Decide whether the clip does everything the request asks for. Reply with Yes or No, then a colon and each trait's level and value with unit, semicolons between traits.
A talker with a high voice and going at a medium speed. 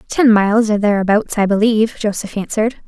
Yes: high, 215 Hz; average, 165 wpm